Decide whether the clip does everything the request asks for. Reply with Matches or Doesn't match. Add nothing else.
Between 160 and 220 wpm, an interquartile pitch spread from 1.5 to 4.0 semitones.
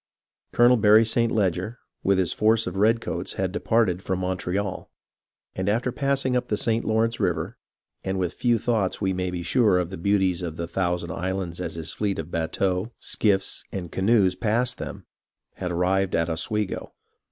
Matches